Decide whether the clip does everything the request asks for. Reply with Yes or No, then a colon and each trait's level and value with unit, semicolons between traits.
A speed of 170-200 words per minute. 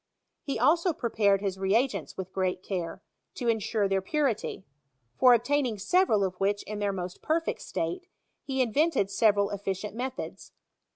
No: average, 150 wpm